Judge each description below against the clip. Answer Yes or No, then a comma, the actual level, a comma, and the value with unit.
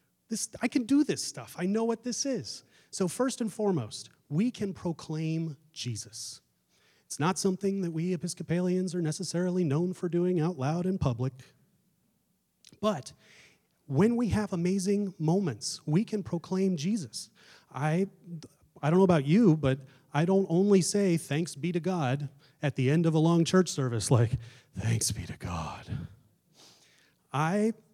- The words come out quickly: No, average, 155 wpm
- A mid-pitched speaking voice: Yes, medium, 175 Hz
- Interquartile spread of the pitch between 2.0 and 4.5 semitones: No, average, 5.0 semitones